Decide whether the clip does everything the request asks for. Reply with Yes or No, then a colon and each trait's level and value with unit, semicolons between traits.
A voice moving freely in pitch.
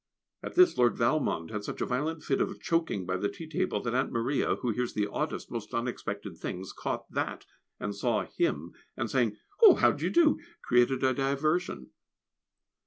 Yes: wide, 6.8 semitones